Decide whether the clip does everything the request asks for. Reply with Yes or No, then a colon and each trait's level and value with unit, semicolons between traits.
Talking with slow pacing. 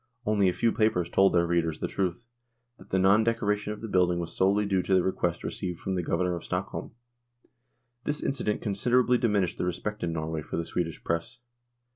No: average, 200 wpm